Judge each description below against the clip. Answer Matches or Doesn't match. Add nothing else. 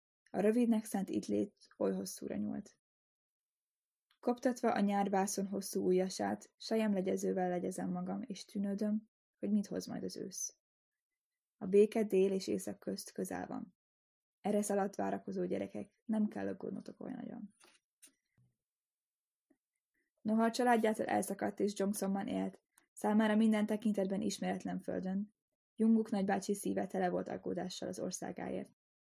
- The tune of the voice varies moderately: Matches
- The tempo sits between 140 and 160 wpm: Doesn't match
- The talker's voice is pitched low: Doesn't match